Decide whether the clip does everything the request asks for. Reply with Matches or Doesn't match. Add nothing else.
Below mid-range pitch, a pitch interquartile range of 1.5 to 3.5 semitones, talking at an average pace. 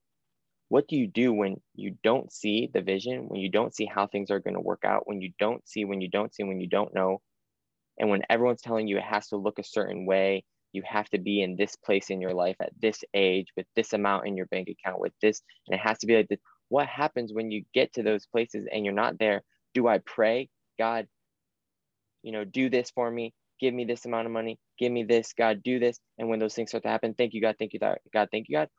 Doesn't match